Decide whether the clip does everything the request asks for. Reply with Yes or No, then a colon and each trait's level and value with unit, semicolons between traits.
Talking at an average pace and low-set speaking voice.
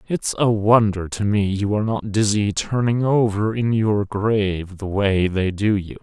Yes: average, 190 wpm; low, 105 Hz